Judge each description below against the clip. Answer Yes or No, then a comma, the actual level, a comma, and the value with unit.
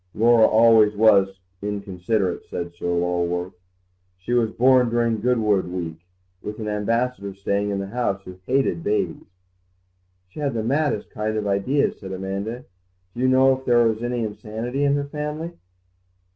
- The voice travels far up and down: No, average, 4.0 semitones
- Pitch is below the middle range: Yes, low, 110 Hz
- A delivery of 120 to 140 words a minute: No, average, 160 wpm